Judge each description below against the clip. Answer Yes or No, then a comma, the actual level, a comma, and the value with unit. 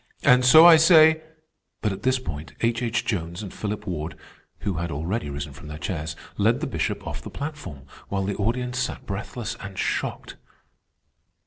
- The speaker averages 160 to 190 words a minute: Yes, average, 180 wpm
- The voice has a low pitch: Yes, low, 105 Hz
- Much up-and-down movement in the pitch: Yes, wide, 7.3 semitones